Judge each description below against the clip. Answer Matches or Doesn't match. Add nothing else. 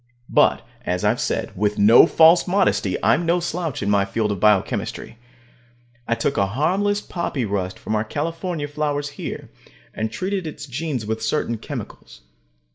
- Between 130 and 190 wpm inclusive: Matches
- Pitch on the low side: Matches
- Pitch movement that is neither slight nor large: Doesn't match